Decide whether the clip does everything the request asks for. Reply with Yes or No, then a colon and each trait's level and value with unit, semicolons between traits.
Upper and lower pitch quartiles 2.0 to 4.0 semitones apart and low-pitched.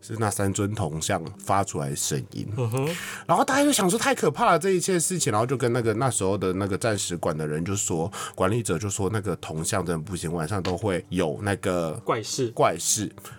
No: average, 4.7 semitones; low, 100 Hz